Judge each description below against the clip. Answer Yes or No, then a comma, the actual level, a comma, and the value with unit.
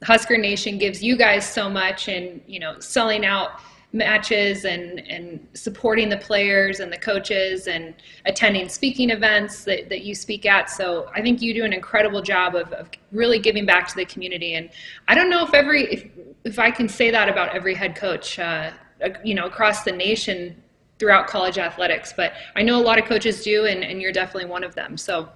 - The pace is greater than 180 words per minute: Yes, fast, 205 wpm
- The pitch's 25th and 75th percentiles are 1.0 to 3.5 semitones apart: Yes, average, 2.9 semitones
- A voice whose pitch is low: No, high, 205 Hz